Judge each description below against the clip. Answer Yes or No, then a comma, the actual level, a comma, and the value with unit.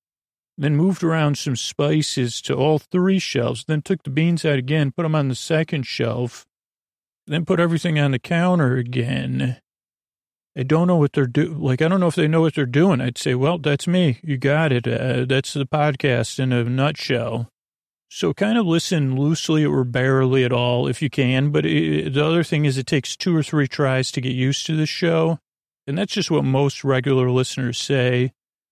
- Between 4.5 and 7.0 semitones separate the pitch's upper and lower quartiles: No, average, 3.8 semitones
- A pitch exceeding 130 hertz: Yes, medium, 140 Hz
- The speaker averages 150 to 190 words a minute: No, fast, 205 wpm